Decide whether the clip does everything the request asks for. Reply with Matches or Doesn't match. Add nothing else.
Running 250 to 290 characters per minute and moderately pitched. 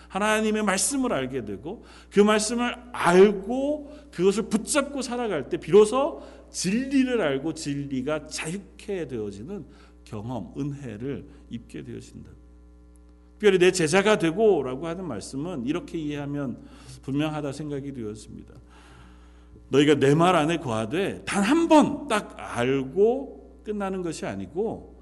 Matches